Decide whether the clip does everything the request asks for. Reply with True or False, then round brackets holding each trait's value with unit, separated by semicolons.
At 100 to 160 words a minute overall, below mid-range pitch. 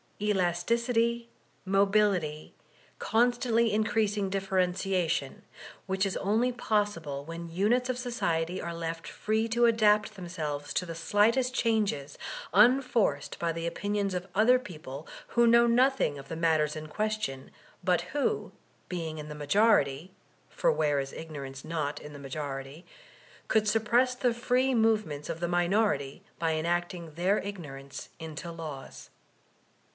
False (135 wpm; 185 Hz)